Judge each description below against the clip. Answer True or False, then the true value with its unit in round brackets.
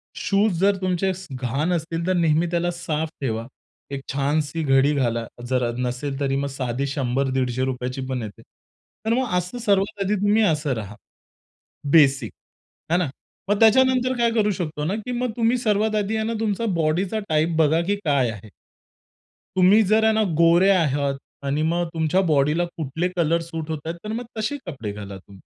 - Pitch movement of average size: False (6.4 semitones)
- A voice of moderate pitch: True (165 Hz)